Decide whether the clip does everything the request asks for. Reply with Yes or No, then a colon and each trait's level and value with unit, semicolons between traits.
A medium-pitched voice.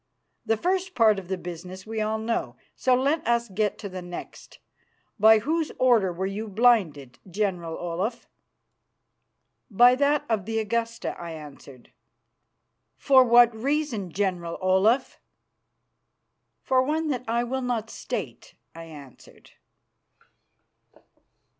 No: high, 220 Hz